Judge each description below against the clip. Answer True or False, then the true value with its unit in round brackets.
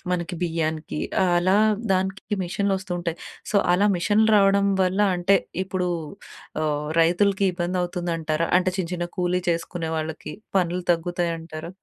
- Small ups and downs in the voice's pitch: True (2.2 semitones)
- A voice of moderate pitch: True (175 Hz)